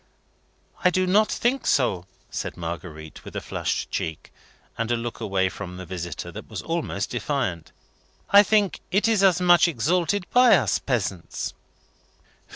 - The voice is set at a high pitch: No, low, 135 Hz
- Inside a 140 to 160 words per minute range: Yes, average, 155 wpm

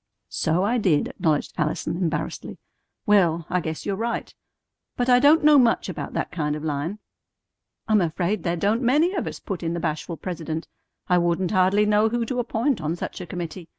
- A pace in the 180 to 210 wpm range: Yes, average, 190 wpm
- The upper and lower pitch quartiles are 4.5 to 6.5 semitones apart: Yes, wide, 5.5 semitones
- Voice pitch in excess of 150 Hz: Yes, medium, 185 Hz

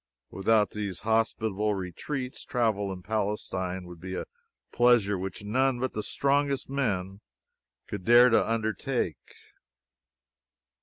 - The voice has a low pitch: Yes, low, 105 Hz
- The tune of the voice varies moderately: Yes, average, 4.1 semitones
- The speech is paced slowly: Yes, slow, 115 wpm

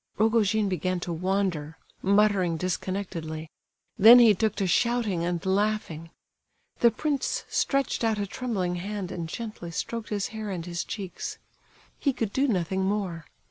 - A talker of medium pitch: No, high, 195 Hz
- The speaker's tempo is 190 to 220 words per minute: No, average, 140 wpm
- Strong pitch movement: No, average, 3.8 semitones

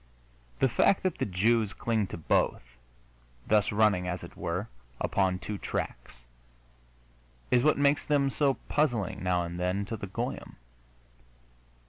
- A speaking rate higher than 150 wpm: No, average, 140 wpm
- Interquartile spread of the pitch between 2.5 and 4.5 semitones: No, average, 5.2 semitones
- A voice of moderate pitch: No, low, 105 Hz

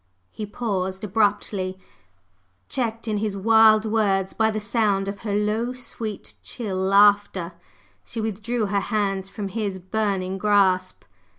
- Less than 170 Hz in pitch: No, high, 205 Hz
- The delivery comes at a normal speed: No, slow, 130 wpm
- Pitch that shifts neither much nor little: No, narrow, 2.1 semitones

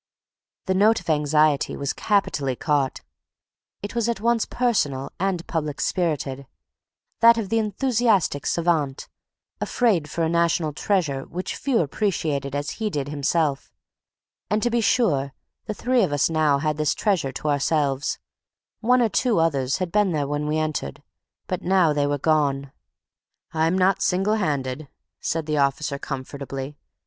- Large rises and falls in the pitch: Yes, wide, 5.8 semitones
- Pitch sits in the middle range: Yes, medium, 155 Hz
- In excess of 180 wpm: No, average, 155 wpm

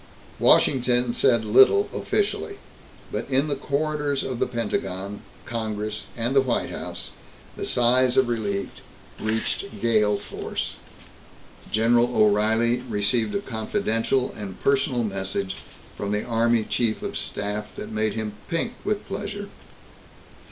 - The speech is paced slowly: Yes, slow, 125 wpm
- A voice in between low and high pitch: No, low, 115 Hz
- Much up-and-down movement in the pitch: No, average, 3.6 semitones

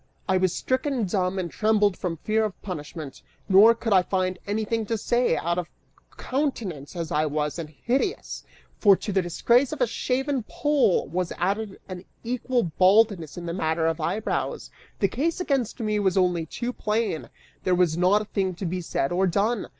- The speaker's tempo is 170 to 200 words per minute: Yes, average, 185 wpm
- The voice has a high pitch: Yes, high, 195 Hz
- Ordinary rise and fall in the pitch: Yes, average, 4.5 semitones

